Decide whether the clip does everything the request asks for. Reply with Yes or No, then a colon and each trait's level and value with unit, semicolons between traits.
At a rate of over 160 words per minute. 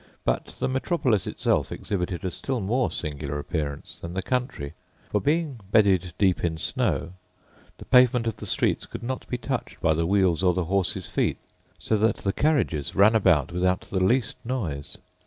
Yes: average, 175 wpm